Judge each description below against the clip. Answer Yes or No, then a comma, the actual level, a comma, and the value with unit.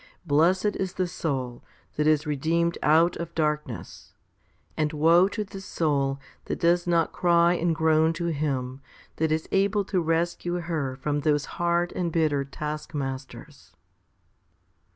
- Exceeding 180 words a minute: No, average, 145 wpm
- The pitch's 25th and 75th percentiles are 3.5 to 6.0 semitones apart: No, average, 2.7 semitones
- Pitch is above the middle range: No, medium, 160 Hz